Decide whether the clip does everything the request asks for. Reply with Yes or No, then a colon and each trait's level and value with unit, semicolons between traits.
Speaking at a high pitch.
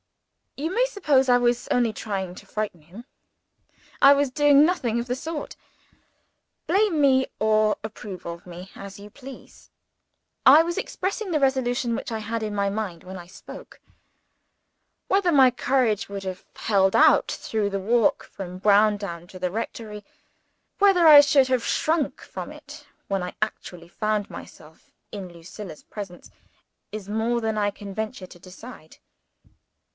Yes: high, 220 Hz